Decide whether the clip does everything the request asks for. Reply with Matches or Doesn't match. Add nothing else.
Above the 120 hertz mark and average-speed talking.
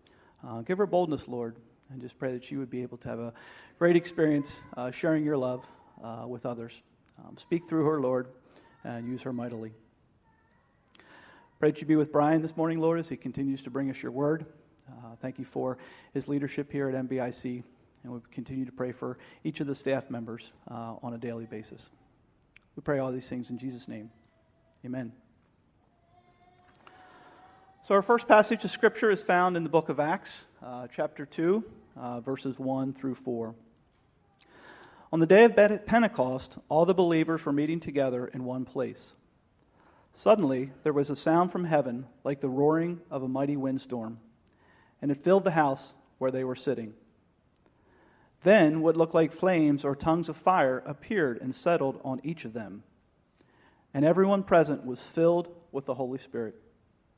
Matches